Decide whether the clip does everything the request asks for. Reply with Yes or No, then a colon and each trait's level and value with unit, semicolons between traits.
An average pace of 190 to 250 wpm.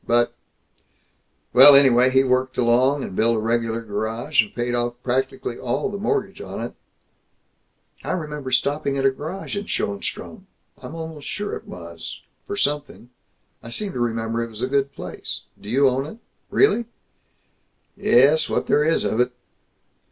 No: average, 170 wpm